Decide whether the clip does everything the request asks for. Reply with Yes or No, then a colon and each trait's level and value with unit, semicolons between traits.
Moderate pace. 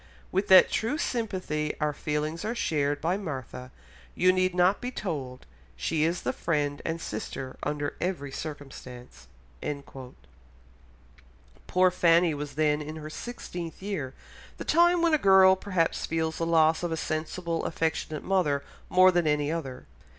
Yes: average, 150 wpm